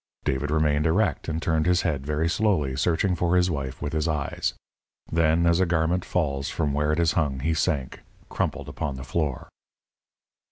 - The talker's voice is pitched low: Yes, very low, 80 Hz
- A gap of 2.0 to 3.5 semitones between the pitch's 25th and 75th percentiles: Yes, average, 2.9 semitones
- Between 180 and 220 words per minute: Yes, average, 185 wpm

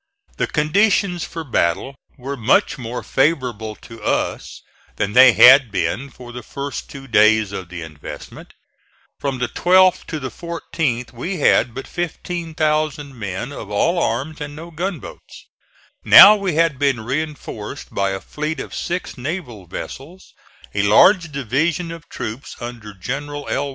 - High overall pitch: No, medium, 140 Hz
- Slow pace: No, average, 150 wpm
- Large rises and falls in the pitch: Yes, wide, 5.8 semitones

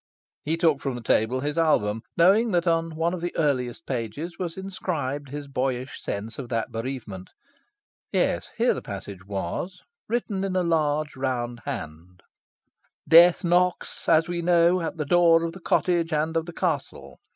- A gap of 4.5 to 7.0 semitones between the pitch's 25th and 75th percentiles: Yes, wide, 5.4 semitones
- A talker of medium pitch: Yes, medium, 155 Hz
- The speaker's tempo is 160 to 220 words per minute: Yes, average, 170 wpm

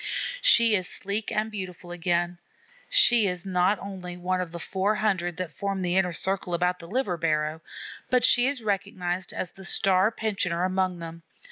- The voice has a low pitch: No, medium, 185 Hz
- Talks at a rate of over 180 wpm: No, average, 175 wpm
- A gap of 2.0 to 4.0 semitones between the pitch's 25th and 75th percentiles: Yes, narrow, 2.4 semitones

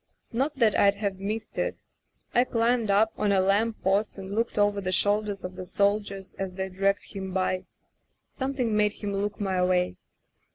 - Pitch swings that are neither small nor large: No, narrow, 2.0 semitones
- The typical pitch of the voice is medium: No, high, 200 Hz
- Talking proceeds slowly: No, average, 180 wpm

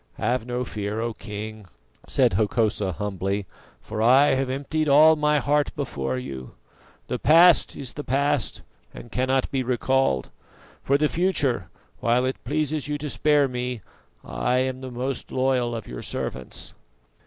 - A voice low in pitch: Yes, low, 125 Hz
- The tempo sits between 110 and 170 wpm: Yes, average, 155 wpm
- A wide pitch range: No, average, 4.5 semitones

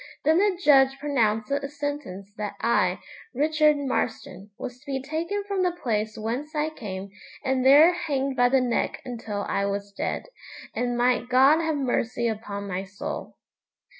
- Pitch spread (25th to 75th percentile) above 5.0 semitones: Yes, wide, 5.5 semitones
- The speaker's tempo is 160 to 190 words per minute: Yes, average, 165 wpm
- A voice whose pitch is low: No, very high, 260 Hz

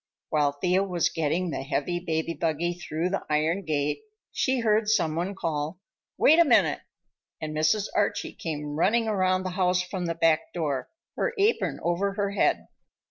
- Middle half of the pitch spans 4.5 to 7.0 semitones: No, average, 4.0 semitones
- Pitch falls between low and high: Yes, medium, 175 Hz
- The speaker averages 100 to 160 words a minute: No, average, 170 wpm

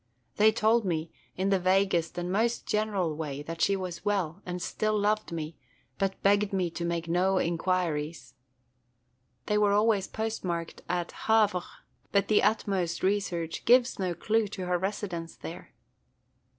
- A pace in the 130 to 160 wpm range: Yes, average, 150 wpm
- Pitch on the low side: No, medium, 185 Hz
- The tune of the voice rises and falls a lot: No, average, 3.4 semitones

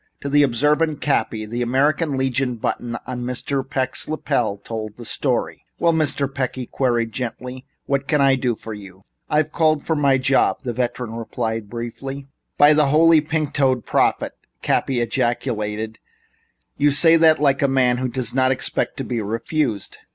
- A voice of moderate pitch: No, low, 130 Hz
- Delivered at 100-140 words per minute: No, average, 165 wpm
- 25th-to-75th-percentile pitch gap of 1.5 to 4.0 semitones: Yes, average, 3.6 semitones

